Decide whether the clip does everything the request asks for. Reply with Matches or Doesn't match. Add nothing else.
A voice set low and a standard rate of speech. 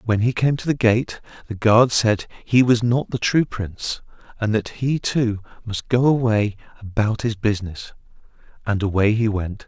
Matches